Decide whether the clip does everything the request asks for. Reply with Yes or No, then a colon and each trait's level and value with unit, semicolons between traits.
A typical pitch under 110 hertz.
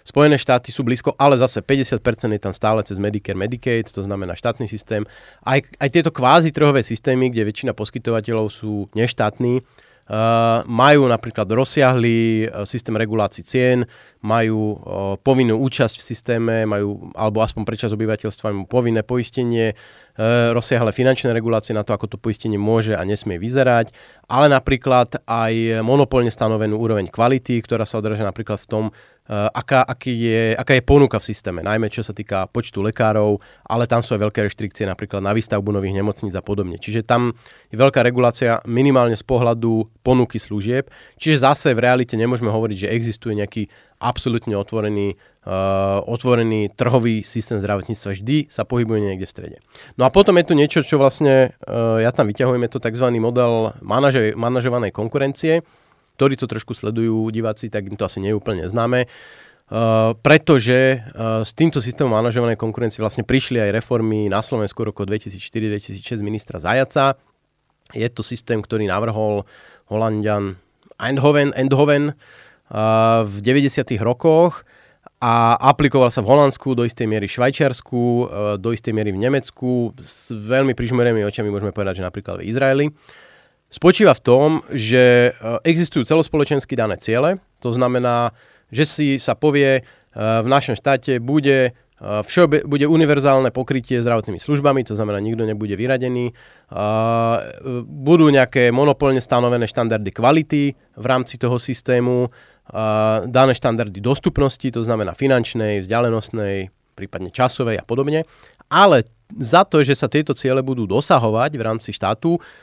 No: low, 115 Hz